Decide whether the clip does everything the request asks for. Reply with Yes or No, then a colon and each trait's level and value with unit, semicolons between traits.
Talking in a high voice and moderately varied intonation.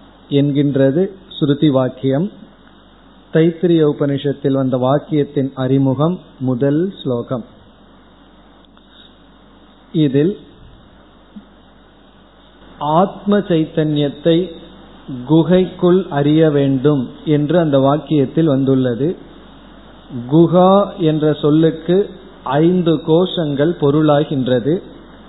No: medium, 150 Hz; average, 3.7 semitones